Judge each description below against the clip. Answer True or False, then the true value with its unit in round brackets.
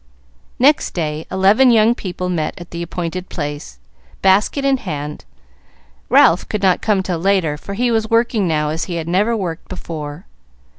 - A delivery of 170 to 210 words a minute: False (160 wpm)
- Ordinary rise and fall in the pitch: True (4.6 semitones)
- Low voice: False (185 Hz)